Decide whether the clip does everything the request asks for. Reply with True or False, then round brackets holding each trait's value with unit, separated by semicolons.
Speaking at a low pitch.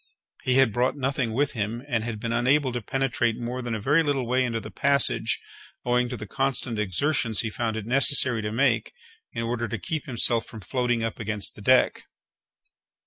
True (120 Hz)